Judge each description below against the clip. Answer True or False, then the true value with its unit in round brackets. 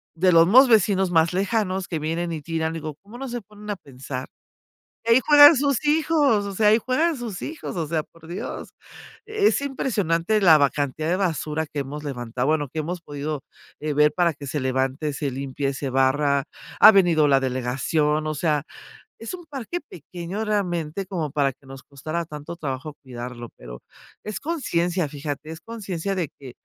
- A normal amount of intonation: False (5.9 semitones)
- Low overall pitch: False (165 Hz)